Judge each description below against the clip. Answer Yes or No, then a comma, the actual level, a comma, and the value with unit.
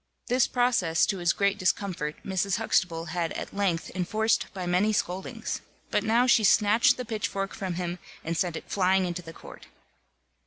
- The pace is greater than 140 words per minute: Yes, average, 170 wpm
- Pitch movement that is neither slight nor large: Yes, average, 3.3 semitones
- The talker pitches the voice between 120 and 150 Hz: No, high, 190 Hz